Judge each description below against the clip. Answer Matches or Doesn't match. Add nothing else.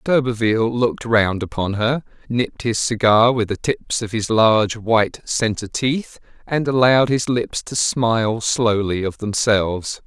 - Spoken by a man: Matches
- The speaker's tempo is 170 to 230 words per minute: Doesn't match